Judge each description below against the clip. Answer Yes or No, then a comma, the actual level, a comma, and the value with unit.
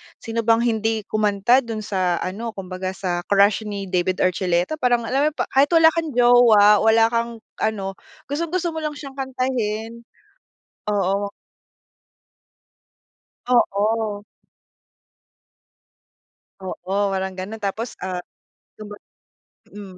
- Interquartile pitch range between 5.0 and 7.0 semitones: No, average, 3.7 semitones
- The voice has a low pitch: No, high, 220 Hz